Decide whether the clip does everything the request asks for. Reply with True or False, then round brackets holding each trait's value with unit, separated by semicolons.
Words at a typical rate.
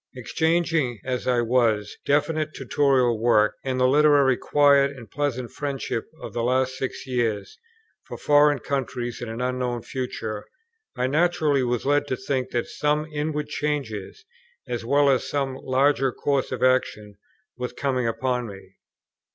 True (150 wpm)